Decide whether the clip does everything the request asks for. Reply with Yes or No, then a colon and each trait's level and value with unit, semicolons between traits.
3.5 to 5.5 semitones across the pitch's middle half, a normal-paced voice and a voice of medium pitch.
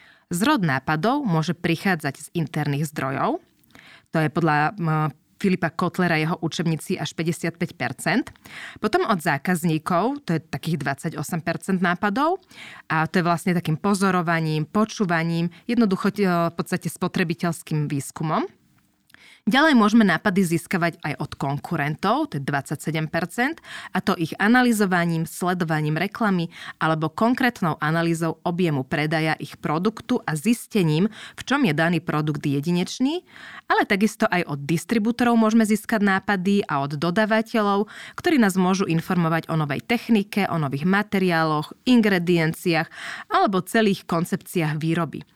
Yes: average, 4.4 semitones; average, 125 wpm; medium, 175 Hz